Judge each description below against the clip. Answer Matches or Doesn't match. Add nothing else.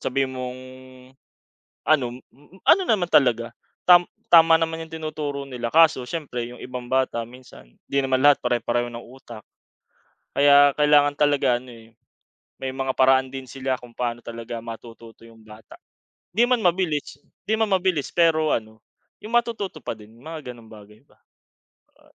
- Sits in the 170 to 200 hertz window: Doesn't match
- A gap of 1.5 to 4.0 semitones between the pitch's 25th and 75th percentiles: Doesn't match